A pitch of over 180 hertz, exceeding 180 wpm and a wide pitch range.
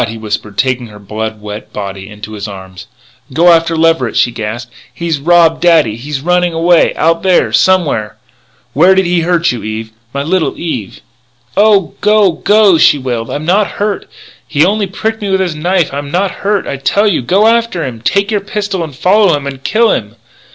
No: medium, 165 Hz; average, 200 wpm; wide, 8.0 semitones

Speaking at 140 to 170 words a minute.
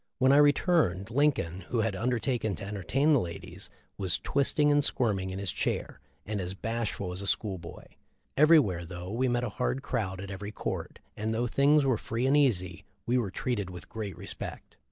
No: average, 195 wpm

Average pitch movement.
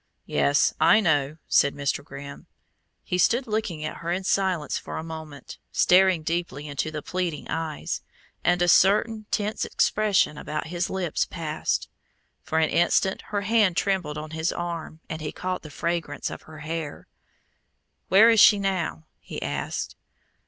Yes: average, 3.7 semitones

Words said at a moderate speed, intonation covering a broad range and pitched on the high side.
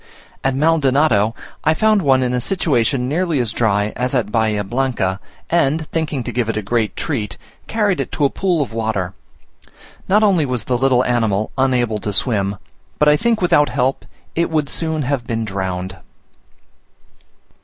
No: average, 170 wpm; wide, 5.7 semitones; low, 125 Hz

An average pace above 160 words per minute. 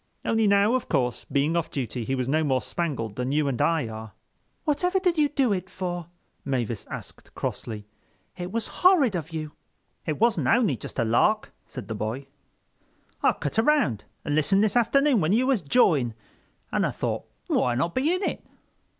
Yes: average, 185 wpm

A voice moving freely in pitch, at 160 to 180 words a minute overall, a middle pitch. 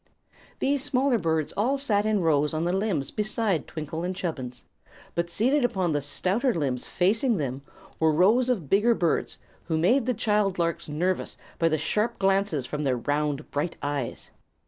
Yes: wide, 6.2 semitones; average, 170 wpm; medium, 180 Hz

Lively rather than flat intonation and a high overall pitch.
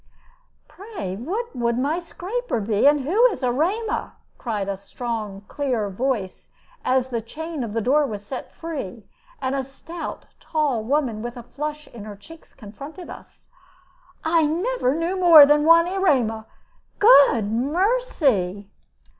Yes: wide, 6.8 semitones; very high, 275 Hz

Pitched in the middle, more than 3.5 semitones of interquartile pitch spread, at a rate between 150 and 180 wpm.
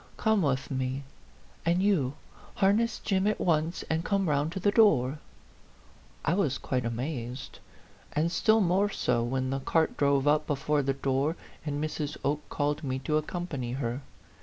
Yes: medium, 150 Hz; average, 4.7 semitones; average, 160 wpm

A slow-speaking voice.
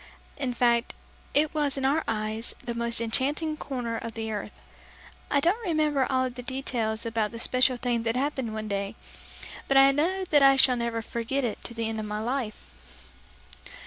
No: average, 185 wpm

